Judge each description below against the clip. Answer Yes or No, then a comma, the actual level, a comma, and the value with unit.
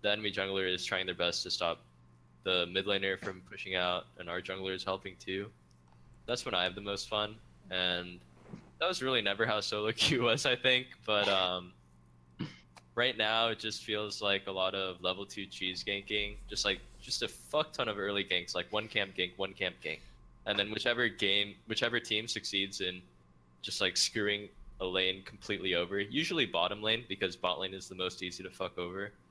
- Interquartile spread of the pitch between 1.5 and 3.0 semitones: Yes, narrow, 2.4 semitones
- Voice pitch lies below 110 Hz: Yes, very low, 95 Hz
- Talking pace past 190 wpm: Yes, average, 200 wpm